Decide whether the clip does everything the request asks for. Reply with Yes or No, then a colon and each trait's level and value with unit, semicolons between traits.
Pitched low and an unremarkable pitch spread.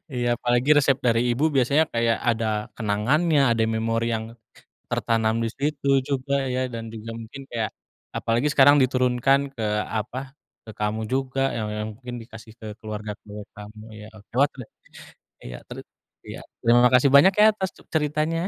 Yes: low, 120 Hz; average, 3.7 semitones